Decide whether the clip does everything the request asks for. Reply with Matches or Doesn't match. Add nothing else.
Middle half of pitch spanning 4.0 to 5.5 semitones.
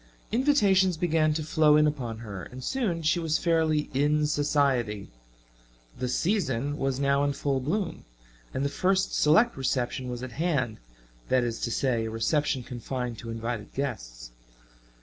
Matches